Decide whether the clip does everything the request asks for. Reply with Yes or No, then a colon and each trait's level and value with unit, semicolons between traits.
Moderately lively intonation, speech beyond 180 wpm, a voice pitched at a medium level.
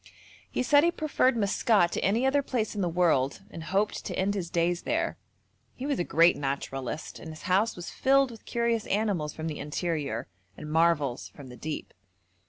No: wide, 6.6 semitones; average, 190 wpm; medium, 175 Hz